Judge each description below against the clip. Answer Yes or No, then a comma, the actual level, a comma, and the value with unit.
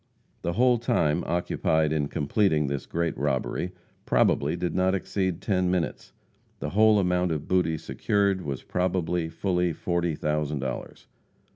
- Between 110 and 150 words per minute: Yes, average, 140 wpm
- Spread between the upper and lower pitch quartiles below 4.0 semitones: Yes, average, 3.4 semitones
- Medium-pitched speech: No, very low, 85 Hz